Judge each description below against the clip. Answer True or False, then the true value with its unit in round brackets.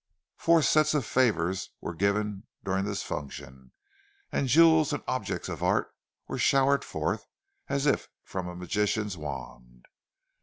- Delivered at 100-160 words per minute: True (140 wpm)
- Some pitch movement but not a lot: False (8.7 semitones)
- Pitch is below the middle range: True (105 Hz)